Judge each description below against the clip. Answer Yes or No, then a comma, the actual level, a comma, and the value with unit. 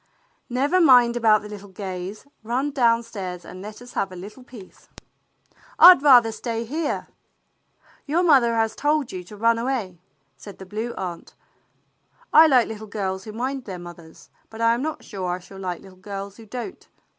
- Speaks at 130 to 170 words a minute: No, average, 185 wpm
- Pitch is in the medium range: No, high, 220 Hz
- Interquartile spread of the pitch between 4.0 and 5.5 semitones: Yes, average, 4.5 semitones